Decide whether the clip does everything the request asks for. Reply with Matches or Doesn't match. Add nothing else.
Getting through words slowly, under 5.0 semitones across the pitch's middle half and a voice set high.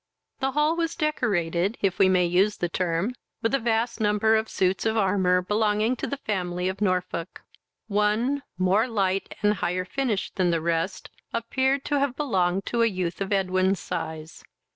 Doesn't match